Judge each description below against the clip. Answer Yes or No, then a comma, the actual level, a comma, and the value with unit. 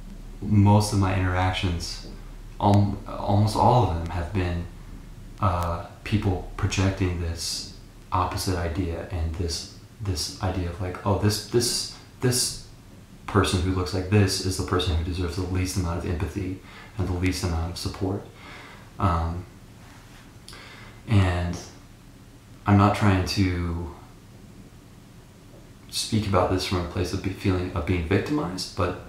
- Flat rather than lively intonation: Yes, narrow, 2.2 semitones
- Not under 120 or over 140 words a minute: Yes, slow, 135 wpm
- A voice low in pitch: Yes, very low, 95 Hz